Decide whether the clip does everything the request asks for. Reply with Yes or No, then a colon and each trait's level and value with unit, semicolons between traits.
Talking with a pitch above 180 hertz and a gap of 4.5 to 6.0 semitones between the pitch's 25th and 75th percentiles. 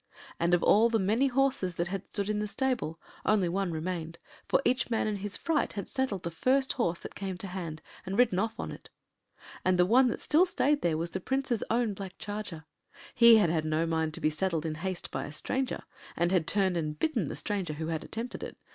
Yes: high, 190 Hz; wide, 5.6 semitones